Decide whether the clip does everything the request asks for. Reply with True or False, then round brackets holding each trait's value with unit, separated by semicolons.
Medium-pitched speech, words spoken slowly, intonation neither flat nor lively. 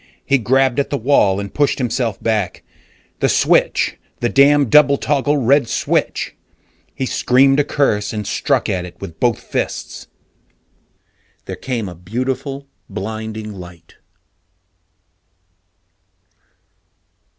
False (120 Hz; 115 wpm; 4.9 semitones)